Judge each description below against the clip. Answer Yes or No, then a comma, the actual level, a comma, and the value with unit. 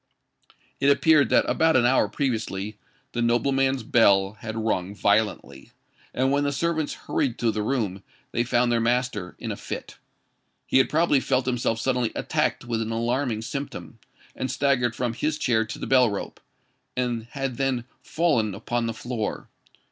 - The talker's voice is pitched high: No, low, 120 Hz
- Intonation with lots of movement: No, average, 3.2 semitones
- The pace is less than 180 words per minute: Yes, average, 165 wpm